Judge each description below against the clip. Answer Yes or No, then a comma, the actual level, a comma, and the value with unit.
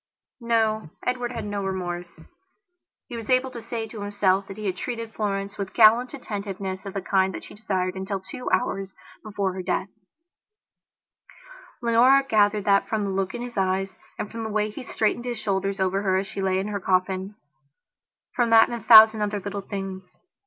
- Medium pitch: No, high, 205 Hz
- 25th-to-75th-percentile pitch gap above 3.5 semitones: No, average, 2.7 semitones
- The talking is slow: No, average, 190 wpm